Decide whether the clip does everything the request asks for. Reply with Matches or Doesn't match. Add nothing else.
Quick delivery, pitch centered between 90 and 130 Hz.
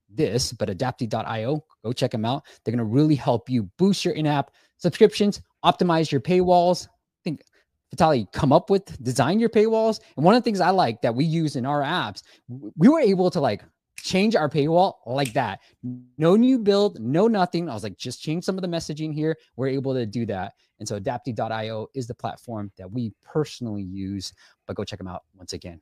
Doesn't match